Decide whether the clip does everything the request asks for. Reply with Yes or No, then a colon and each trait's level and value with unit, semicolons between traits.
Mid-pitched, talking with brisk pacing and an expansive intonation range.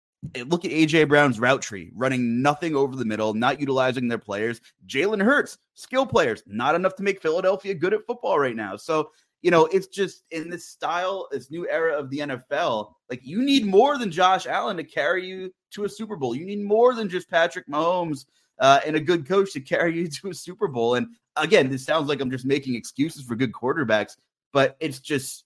Yes: medium, 160 Hz; fast, 215 wpm; wide, 6.1 semitones